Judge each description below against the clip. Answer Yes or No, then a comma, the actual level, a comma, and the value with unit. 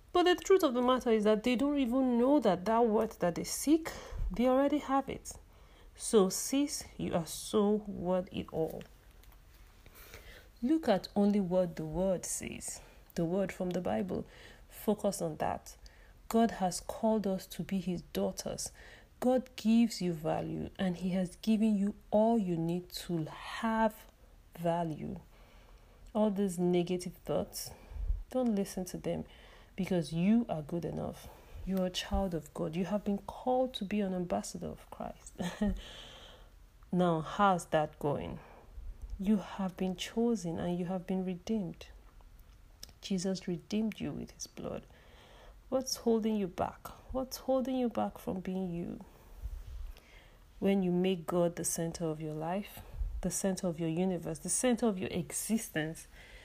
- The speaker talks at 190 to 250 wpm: No, average, 155 wpm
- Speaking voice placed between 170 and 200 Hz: Yes, high, 190 Hz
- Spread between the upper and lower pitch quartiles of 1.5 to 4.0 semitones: No, average, 4.4 semitones